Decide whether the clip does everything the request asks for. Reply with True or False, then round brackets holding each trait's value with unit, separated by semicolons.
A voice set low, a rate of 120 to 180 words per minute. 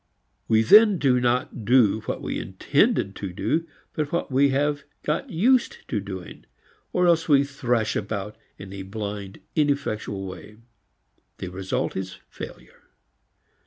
True (120 Hz; 140 wpm)